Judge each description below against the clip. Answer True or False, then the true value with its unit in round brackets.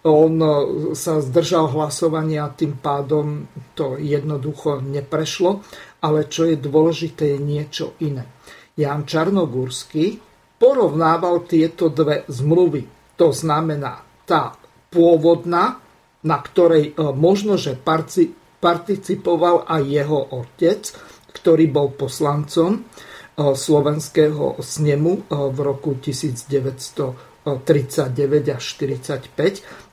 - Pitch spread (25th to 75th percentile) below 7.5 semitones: True (2.5 semitones)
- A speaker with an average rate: False (90 wpm)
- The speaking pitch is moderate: True (155 Hz)